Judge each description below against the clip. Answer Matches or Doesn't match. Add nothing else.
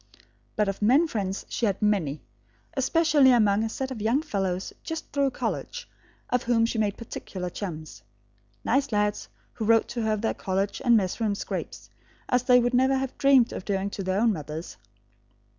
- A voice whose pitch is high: Matches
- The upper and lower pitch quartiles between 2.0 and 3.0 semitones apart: Doesn't match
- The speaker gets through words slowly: Doesn't match